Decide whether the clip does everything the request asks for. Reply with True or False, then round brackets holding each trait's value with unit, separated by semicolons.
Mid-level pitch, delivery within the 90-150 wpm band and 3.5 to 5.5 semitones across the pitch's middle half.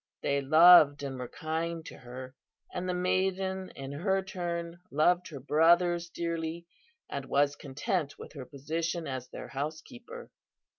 True (165 Hz; 145 wpm; 4.0 semitones)